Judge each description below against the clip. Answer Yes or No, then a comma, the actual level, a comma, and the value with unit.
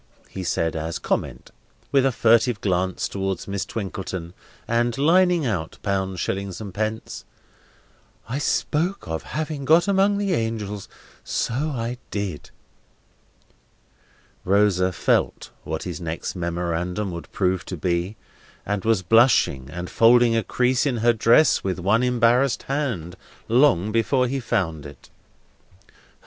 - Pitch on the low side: Yes, low, 105 Hz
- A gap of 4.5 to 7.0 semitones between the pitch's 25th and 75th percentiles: Yes, wide, 5.4 semitones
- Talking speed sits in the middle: No, slow, 130 wpm